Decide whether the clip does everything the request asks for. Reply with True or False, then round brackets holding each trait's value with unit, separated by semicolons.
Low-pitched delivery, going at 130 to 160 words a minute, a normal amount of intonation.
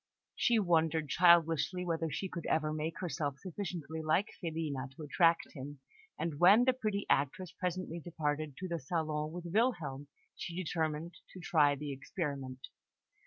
False (165 Hz; 150 wpm; 3.2 semitones)